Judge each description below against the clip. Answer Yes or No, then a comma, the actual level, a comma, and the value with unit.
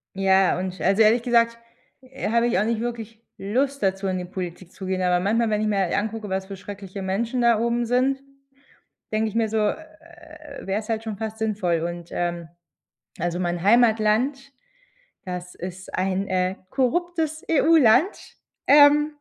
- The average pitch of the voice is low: No, high, 215 Hz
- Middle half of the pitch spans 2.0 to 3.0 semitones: No, average, 4.0 semitones